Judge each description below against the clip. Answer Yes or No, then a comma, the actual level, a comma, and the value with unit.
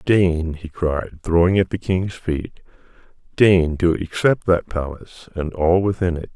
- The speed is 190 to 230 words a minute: No, average, 160 wpm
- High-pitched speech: No, very low, 85 Hz